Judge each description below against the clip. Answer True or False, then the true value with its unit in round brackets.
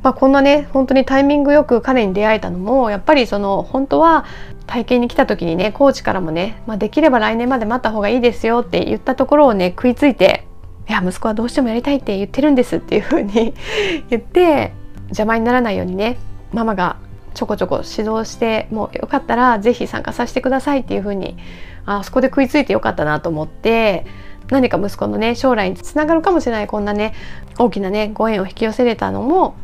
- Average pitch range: True (4.7 semitones)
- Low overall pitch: False (230 Hz)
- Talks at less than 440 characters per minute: False (445 characters per minute)